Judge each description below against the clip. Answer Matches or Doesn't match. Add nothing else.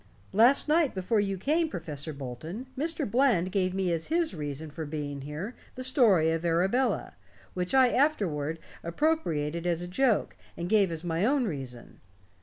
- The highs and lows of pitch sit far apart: Matches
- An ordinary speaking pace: Matches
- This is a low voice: Doesn't match